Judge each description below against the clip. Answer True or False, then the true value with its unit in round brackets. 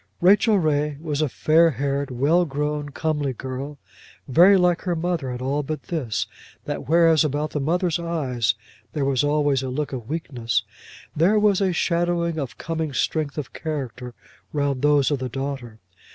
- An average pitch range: True (3.6 semitones)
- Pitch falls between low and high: True (150 Hz)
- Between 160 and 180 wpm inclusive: True (165 wpm)